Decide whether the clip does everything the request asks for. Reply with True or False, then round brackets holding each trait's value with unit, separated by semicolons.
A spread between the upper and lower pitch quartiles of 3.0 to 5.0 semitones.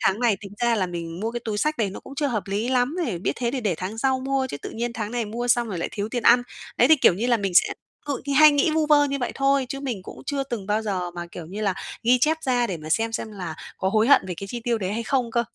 True (4.7 semitones)